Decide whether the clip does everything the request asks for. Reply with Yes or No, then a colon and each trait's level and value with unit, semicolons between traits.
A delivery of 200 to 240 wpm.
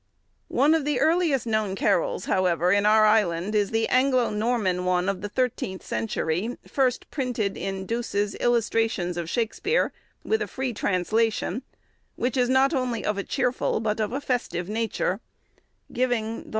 No: average, 160 wpm